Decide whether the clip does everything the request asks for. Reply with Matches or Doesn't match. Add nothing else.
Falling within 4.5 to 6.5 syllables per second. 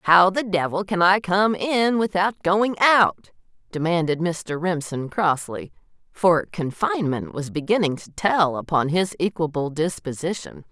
Doesn't match